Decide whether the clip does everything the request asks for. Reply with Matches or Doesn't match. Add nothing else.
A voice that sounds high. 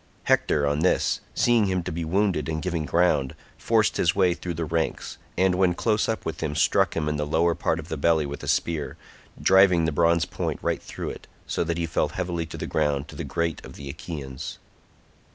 Doesn't match